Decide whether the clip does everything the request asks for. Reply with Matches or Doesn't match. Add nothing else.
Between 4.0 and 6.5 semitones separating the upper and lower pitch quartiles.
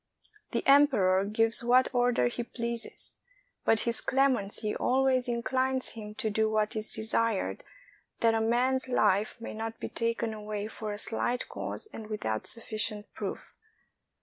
Doesn't match